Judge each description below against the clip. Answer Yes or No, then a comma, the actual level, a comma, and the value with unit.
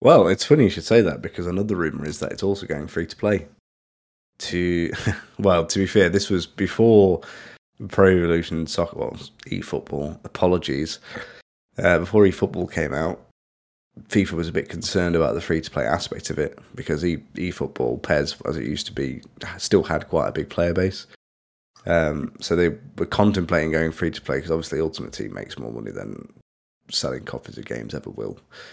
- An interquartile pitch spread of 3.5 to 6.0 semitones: No, average, 2.9 semitones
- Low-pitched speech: Yes, very low, 85 Hz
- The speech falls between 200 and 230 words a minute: No, average, 185 wpm